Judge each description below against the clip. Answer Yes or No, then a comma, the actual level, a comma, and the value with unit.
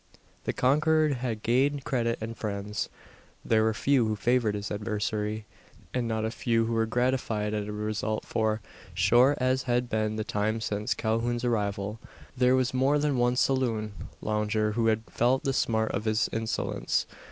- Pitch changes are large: No, average, 2.7 semitones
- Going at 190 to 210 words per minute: No, average, 170 wpm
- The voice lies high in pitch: No, low, 115 Hz